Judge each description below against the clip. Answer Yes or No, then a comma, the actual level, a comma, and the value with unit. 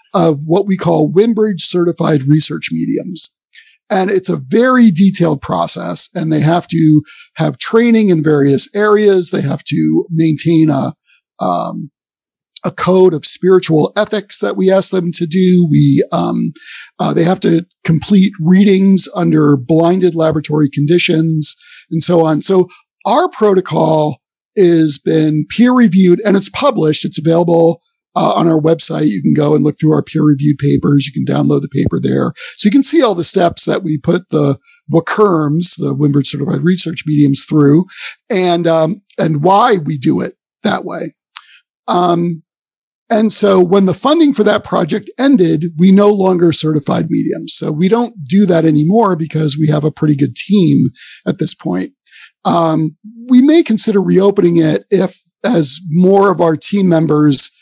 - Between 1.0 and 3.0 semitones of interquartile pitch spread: No, average, 4.0 semitones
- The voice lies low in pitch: No, medium, 170 Hz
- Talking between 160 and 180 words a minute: Yes, average, 165 wpm